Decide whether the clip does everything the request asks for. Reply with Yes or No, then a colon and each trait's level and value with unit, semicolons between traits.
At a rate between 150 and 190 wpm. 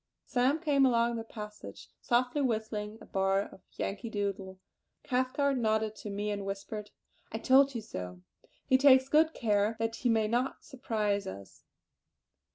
Yes: average, 155 wpm